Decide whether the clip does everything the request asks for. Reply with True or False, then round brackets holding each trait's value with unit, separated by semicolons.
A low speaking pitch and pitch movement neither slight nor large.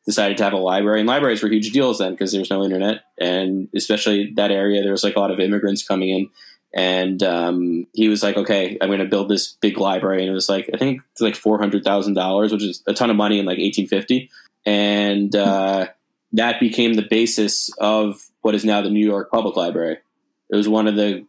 False (100 Hz; 1.7 semitones)